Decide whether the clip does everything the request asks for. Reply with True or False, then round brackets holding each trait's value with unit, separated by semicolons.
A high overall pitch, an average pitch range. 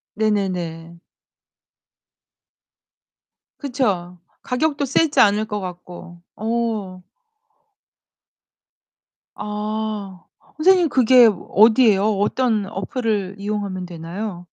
True (210 Hz; 4.1 semitones)